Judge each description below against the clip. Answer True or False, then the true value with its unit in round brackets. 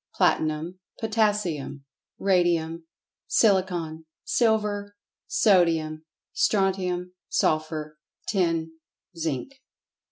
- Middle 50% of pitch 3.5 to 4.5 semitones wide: True (4.2 semitones)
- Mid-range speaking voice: True (175 Hz)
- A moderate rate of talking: False (60 wpm)